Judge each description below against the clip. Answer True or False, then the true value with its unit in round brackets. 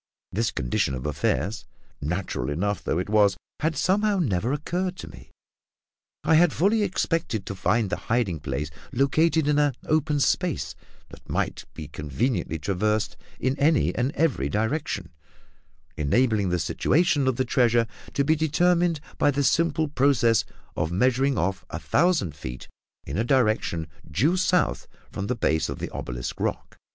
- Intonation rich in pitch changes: True (8.8 semitones)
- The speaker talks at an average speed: True (155 wpm)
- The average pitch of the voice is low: True (125 Hz)